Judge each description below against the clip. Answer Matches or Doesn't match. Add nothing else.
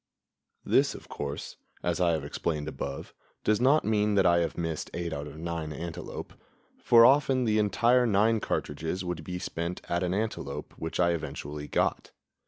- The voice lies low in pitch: Matches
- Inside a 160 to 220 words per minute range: Matches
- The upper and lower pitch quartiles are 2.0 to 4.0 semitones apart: Doesn't match